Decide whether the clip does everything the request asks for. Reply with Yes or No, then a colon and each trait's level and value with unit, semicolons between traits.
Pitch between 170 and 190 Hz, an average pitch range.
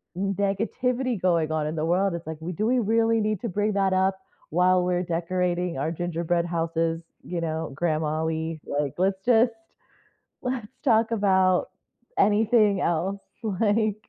Yes: medium, 185 Hz; average, 4.3 semitones